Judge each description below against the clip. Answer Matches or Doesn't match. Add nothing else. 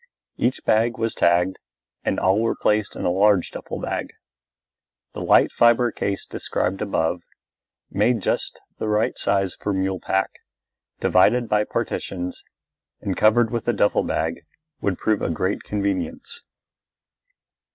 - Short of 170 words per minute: Matches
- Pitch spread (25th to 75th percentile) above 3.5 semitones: Doesn't match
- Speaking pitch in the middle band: Doesn't match